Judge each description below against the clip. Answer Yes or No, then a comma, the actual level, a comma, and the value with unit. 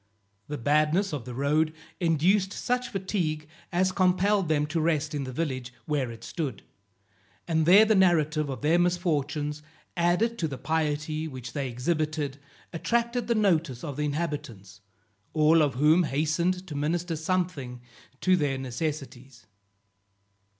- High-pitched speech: No, medium, 155 Hz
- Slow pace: No, average, 145 wpm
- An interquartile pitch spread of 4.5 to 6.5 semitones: No, average, 3.6 semitones